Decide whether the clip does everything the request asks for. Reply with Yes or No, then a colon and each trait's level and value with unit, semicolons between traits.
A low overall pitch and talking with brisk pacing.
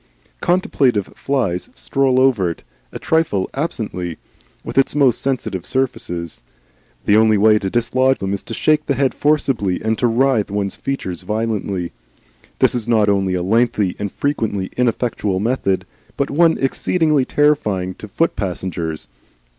No: low, 110 Hz; average, 145 wpm